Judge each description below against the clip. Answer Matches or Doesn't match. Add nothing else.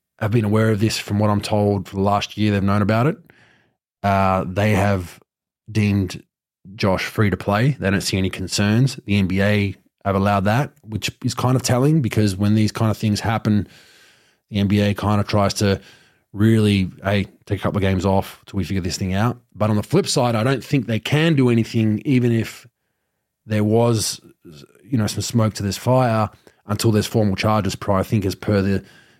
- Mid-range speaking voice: Doesn't match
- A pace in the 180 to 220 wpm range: Matches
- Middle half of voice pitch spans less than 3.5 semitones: Matches